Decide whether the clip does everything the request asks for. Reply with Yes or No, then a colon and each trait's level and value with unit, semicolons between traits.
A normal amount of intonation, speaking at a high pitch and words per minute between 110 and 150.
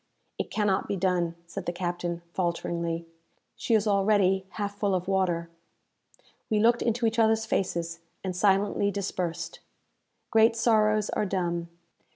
Yes: average, 3.5 semitones; high, 195 Hz; average, 140 wpm